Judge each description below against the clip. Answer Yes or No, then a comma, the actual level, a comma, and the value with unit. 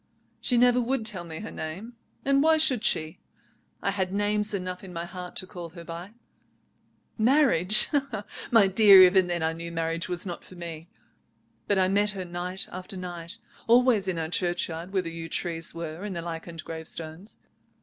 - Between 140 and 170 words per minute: No, average, 180 wpm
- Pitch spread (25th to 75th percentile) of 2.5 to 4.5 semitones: Yes, average, 3.6 semitones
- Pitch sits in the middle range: Yes, medium, 180 Hz